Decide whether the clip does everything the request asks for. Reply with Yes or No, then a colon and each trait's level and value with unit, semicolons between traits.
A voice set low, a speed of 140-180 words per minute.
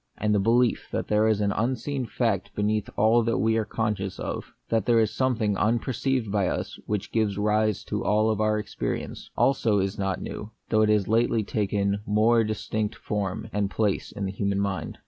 No: low, 105 Hz; fast, 205 wpm